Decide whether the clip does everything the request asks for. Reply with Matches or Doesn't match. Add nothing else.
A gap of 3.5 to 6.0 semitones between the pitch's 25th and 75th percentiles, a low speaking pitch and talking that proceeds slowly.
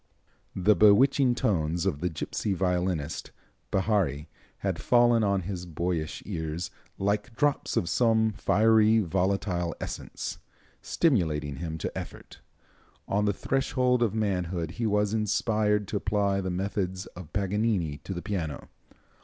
Matches